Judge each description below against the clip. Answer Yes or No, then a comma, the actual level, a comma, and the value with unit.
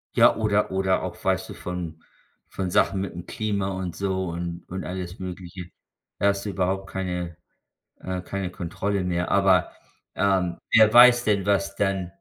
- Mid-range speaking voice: No, very low, 95 Hz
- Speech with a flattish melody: Yes, narrow, 1.8 semitones